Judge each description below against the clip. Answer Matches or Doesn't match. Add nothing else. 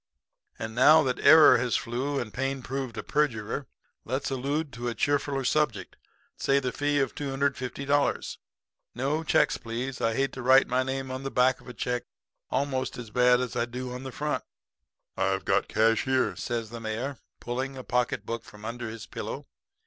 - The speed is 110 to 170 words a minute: Doesn't match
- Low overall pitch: Matches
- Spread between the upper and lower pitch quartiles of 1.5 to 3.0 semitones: Matches